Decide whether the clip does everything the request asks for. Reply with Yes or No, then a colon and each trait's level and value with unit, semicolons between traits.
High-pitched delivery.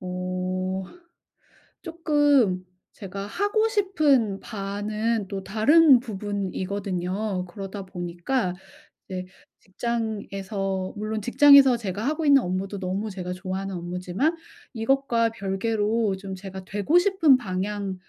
Yes: high, 205 Hz